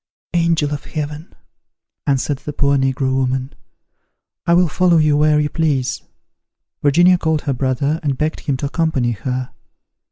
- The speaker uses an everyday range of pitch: Yes, average, 3.0 semitones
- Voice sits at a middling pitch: Yes, medium, 145 Hz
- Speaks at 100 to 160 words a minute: Yes, average, 150 wpm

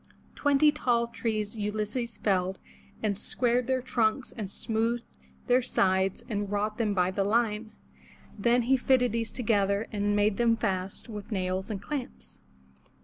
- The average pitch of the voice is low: No, high, 215 Hz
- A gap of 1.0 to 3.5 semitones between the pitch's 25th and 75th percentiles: Yes, average, 2.9 semitones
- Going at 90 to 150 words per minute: Yes, average, 145 wpm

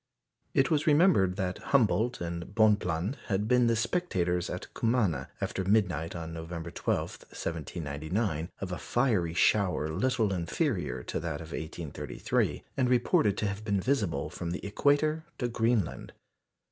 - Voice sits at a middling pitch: No, very low, 95 Hz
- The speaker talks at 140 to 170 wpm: Yes, average, 145 wpm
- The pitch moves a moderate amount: No, wide, 6.0 semitones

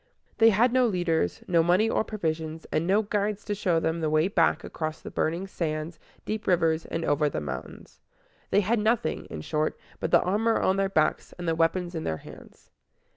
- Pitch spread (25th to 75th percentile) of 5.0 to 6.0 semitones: No, average, 4.4 semitones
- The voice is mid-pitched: Yes, medium, 175 Hz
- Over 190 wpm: Yes, average, 200 wpm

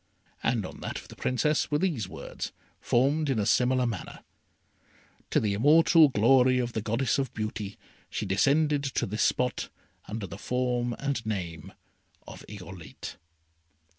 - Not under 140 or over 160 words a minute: Yes, average, 150 wpm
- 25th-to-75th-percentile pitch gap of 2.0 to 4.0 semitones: No, average, 4.4 semitones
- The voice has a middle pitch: No, low, 120 Hz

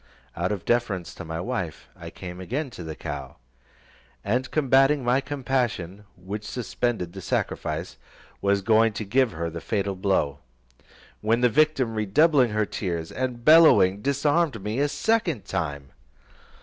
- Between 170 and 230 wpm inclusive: No, average, 150 wpm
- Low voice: Yes, low, 110 Hz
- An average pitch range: No, wide, 6.3 semitones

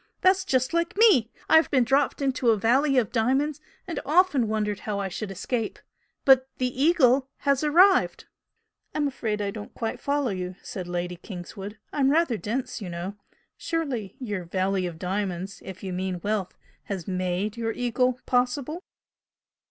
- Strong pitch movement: Yes, wide, 6.1 semitones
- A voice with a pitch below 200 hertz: No, high, 230 Hz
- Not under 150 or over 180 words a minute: Yes, average, 160 wpm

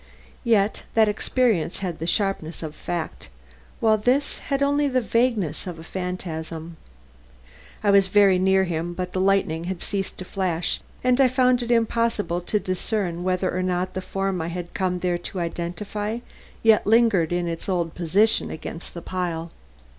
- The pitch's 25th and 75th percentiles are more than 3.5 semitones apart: Yes, average, 3.9 semitones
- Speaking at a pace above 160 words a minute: Yes, average, 170 wpm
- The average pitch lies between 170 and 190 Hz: Yes, medium, 185 Hz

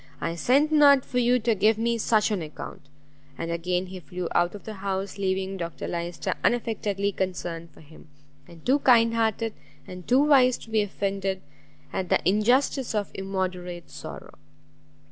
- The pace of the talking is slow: No, average, 165 wpm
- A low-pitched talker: No, high, 200 Hz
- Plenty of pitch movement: No, average, 4.2 semitones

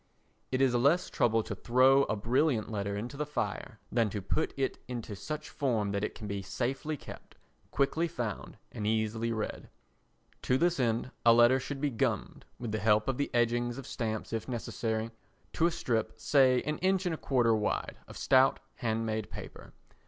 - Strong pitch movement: No, average, 3.7 semitones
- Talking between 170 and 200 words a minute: Yes, average, 190 wpm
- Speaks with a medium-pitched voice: No, low, 120 Hz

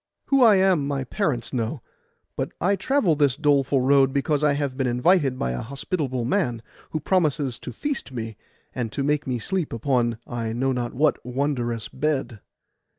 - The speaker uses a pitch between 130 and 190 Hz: Yes, low, 135 Hz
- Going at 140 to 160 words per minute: No, average, 175 wpm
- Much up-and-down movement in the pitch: No, average, 3.8 semitones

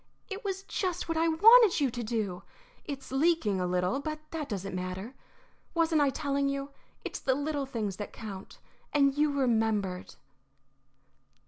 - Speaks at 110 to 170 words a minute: Yes, average, 155 wpm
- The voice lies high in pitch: Yes, very high, 275 Hz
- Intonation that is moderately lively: No, wide, 6.9 semitones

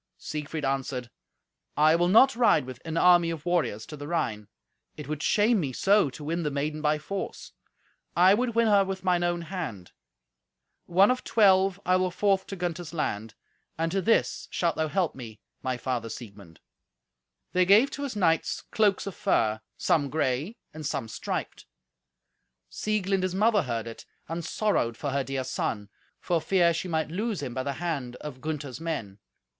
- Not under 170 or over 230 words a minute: Yes, average, 180 wpm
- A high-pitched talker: No, medium, 165 Hz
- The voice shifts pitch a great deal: Yes, wide, 5.9 semitones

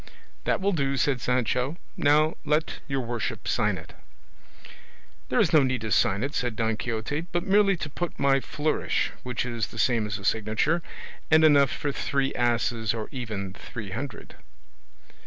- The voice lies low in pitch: Yes, low, 130 Hz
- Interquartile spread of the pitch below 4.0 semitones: No, average, 4.7 semitones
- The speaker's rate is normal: Yes, average, 170 wpm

